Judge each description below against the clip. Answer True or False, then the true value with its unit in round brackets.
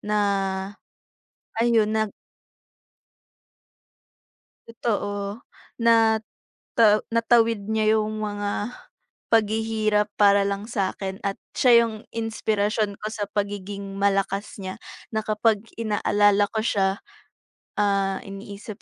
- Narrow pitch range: True (1.7 semitones)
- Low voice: False (210 Hz)